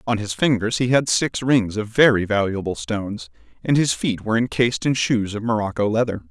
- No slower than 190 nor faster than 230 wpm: Yes, average, 200 wpm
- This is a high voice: No, low, 110 Hz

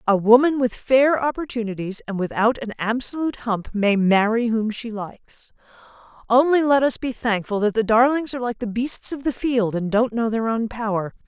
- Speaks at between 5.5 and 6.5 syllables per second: No, 5.1 syllables/s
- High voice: Yes, high, 230 Hz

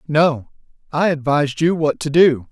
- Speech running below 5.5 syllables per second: Yes, 4.6 syllables/s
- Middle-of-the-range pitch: Yes, medium, 150 Hz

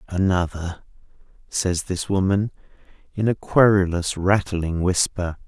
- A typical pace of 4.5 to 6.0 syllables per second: No, 4.0 syllables/s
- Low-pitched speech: Yes, very low, 95 Hz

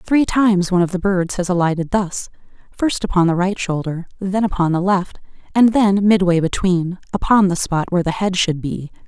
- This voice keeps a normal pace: Yes, average, 185 wpm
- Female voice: Yes, female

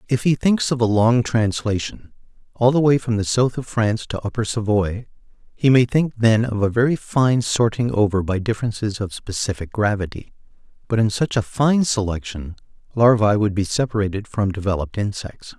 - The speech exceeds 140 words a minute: Yes, average, 170 wpm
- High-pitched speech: No, low, 110 Hz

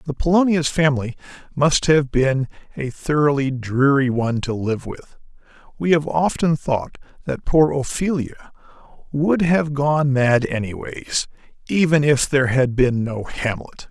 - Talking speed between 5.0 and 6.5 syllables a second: No, 4.7 syllables/s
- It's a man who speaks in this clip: Yes, male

